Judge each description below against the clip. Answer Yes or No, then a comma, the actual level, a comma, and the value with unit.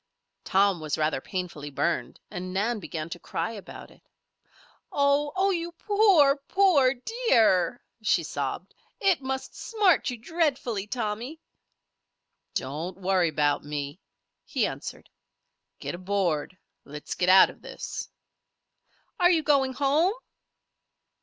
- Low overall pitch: No, high, 225 Hz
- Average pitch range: No, wide, 8.9 semitones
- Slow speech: Yes, slow, 120 wpm